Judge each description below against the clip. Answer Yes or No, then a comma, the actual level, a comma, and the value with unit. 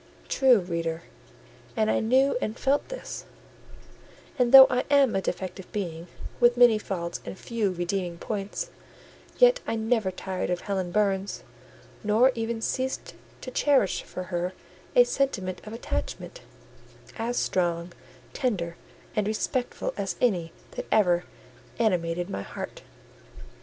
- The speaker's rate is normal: No, slow, 130 wpm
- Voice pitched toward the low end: No, high, 210 Hz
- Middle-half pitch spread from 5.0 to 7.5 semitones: Yes, wide, 5.4 semitones